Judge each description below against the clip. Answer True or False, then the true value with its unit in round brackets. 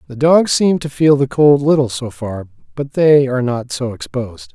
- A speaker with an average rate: False (210 wpm)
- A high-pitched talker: False (135 Hz)